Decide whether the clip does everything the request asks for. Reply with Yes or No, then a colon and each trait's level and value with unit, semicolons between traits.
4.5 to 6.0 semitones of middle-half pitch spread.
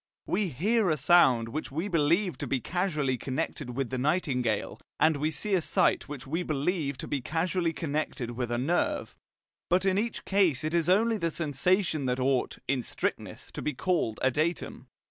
Yes: average, 5.2 semitones